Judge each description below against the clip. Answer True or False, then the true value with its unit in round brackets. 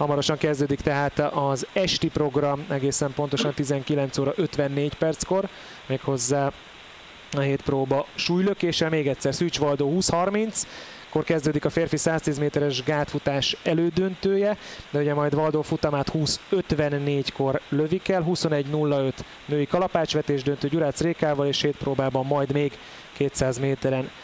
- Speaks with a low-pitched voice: False (145 Hz)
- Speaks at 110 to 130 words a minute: True (125 wpm)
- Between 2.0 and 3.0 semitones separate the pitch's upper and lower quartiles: True (2.6 semitones)